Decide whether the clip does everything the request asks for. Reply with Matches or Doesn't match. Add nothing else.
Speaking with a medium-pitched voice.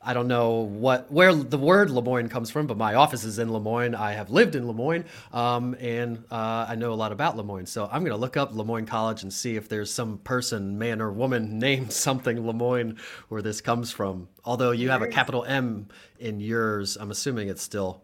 Doesn't match